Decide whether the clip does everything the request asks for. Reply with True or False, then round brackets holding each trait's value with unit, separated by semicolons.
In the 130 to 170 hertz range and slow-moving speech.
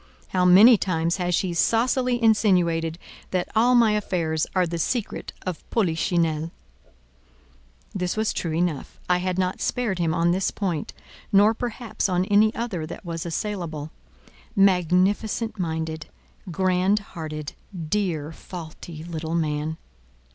False (180 Hz; 130 wpm)